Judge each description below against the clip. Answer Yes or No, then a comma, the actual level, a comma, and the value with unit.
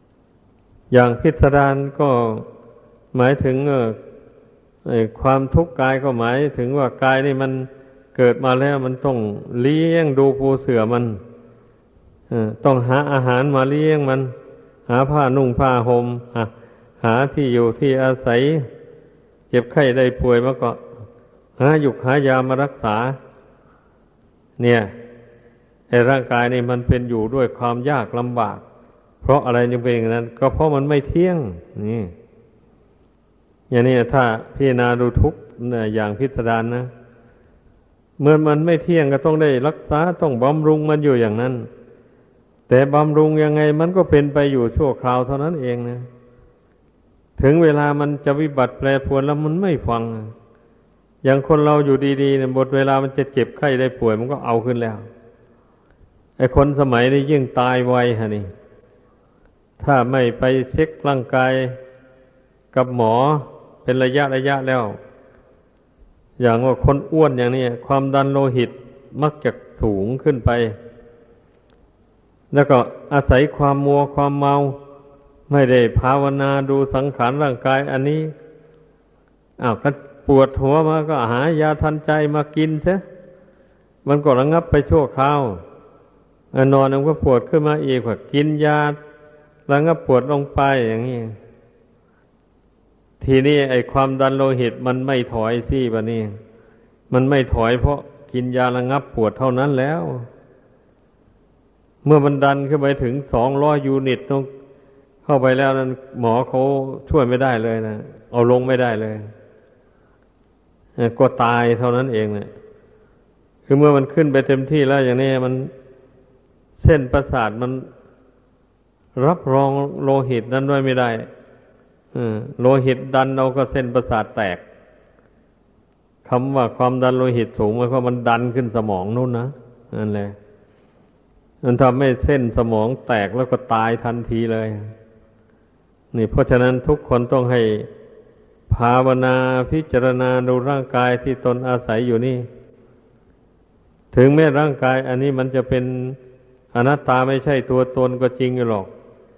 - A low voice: Yes, low, 130 Hz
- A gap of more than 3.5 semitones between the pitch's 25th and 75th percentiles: No, average, 2.7 semitones